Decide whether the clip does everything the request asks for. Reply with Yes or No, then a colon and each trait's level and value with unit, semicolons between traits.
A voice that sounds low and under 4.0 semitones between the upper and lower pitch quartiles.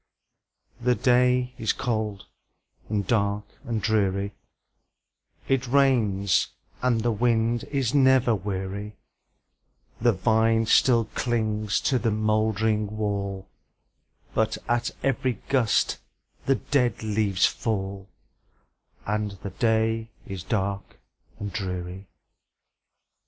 Yes: low, 110 Hz; average, 3.0 semitones